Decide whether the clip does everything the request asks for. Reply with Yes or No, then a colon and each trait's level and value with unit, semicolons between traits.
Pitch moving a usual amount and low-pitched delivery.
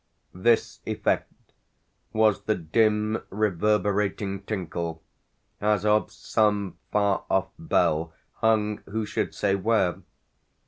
No: narrow, 2.1 semitones; low, 105 Hz